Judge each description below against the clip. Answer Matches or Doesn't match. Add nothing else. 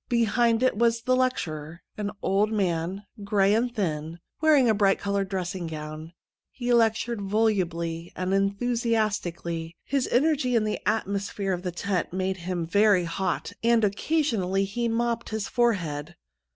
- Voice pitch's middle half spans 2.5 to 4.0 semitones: Doesn't match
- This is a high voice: Matches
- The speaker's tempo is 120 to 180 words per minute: Matches